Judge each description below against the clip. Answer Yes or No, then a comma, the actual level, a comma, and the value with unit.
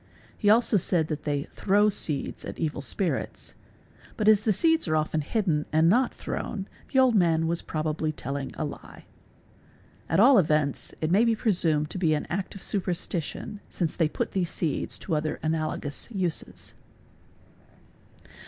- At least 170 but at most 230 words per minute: Yes, average, 180 wpm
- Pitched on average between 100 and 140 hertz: No, medium, 165 Hz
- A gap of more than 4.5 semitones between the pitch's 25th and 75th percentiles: Yes, average, 4.9 semitones